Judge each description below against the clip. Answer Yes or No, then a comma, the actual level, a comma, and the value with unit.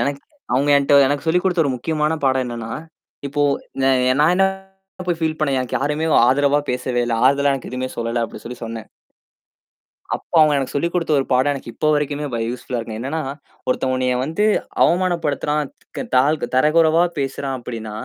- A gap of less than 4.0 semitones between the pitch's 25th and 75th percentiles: Yes, average, 3.3 semitones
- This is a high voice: No, medium, 140 Hz